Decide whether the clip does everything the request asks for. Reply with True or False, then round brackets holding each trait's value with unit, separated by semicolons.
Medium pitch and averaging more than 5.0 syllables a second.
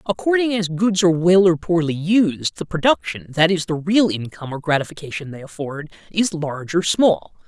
True (170 Hz; 5.3 syllables/s)